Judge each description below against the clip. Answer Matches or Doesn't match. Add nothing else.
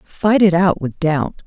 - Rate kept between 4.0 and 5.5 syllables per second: Doesn't match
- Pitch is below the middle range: Doesn't match